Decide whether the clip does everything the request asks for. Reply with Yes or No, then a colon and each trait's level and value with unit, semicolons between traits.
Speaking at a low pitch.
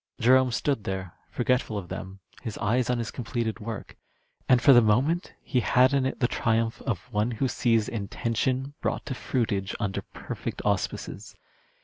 Yes: low, 120 Hz